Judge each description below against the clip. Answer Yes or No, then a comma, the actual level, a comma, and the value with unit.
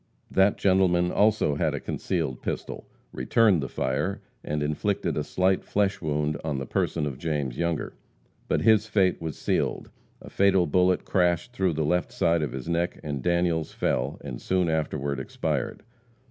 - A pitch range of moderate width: Yes, average, 4.1 semitones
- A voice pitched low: Yes, very low, 85 Hz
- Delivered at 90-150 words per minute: No, average, 165 wpm